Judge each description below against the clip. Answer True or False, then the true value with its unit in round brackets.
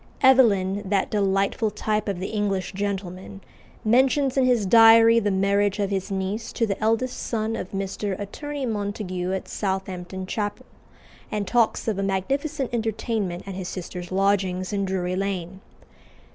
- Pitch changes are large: False (2.7 semitones)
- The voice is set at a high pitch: True (200 Hz)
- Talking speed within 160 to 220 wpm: False (150 wpm)